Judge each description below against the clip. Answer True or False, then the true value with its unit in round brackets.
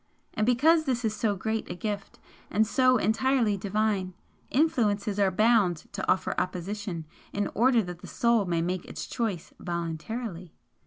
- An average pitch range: True (4.2 semitones)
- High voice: True (210 Hz)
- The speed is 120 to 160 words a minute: True (155 wpm)